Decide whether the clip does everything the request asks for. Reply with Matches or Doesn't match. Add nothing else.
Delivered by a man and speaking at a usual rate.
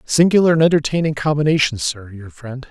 Matches